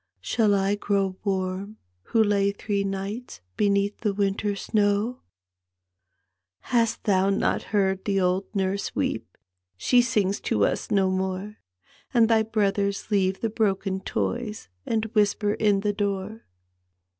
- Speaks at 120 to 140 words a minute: Yes, slow, 135 wpm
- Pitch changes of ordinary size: No, narrow, 1.7 semitones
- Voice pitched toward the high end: Yes, high, 200 Hz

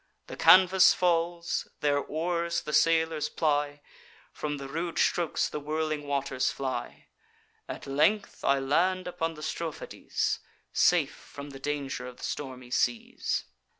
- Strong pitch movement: No, average, 3.3 semitones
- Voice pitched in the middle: Yes, medium, 150 Hz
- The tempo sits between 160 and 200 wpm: No, slow, 135 wpm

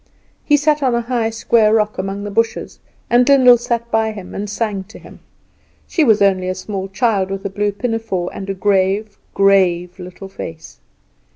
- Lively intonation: No, average, 3.0 semitones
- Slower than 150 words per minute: No, average, 185 wpm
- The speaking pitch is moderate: No, high, 205 Hz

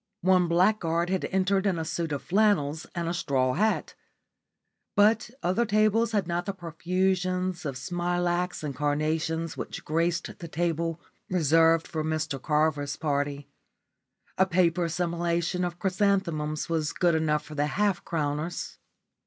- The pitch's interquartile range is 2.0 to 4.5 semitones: Yes, average, 2.8 semitones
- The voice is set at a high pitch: No, medium, 170 Hz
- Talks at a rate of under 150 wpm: Yes, average, 140 wpm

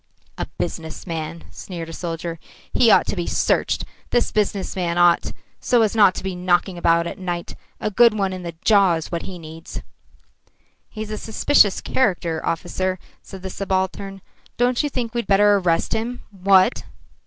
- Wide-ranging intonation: No, average, 3.6 semitones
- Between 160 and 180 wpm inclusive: Yes, average, 175 wpm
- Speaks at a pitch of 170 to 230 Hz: Yes, high, 190 Hz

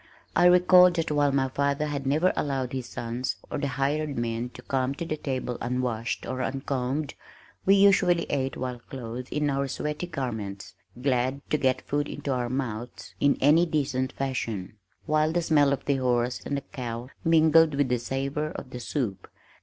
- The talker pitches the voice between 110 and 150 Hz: Yes, low, 135 Hz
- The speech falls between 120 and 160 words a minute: No, average, 180 wpm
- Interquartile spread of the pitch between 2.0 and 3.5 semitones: Yes, average, 3.2 semitones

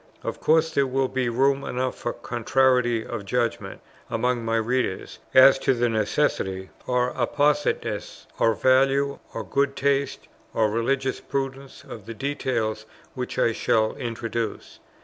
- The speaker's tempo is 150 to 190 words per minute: No, average, 140 wpm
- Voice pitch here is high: No, low, 125 Hz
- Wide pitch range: No, average, 3.0 semitones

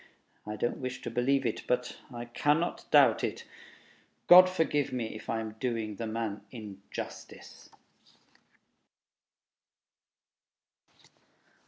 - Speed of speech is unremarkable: No, slow, 110 wpm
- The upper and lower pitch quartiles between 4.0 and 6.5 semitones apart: No, average, 3.3 semitones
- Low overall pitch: Yes, low, 120 Hz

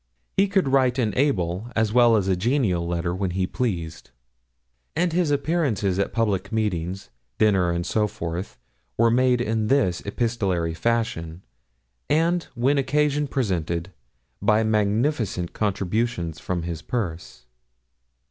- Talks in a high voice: No, low, 105 Hz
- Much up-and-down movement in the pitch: Yes, wide, 6.0 semitones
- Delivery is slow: Yes, slow, 130 wpm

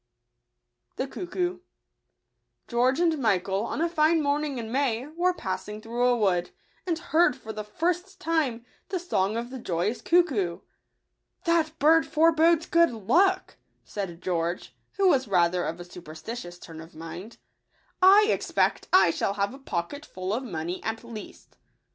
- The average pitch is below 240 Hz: No, high, 245 Hz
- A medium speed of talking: Yes, average, 160 wpm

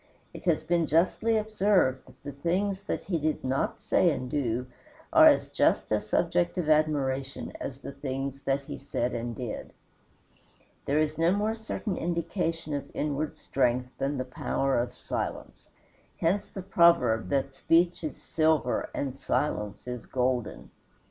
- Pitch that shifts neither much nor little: Yes, average, 4.5 semitones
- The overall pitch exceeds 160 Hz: No, medium, 145 Hz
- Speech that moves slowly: No, average, 155 wpm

